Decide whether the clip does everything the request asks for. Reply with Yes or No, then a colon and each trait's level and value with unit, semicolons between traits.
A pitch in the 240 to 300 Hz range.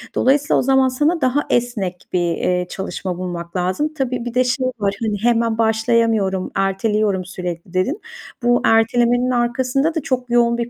No: high, 230 Hz